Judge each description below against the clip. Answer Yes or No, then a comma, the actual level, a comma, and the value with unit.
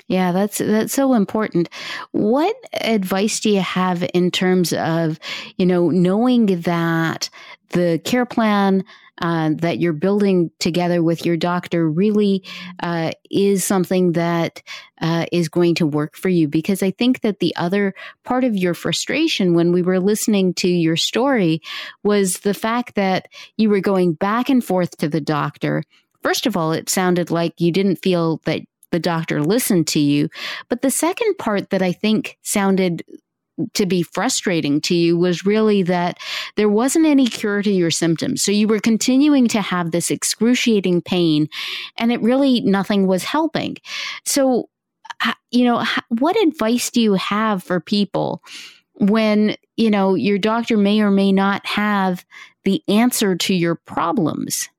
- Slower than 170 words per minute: Yes, average, 160 wpm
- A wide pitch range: No, average, 4.4 semitones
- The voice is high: Yes, high, 195 Hz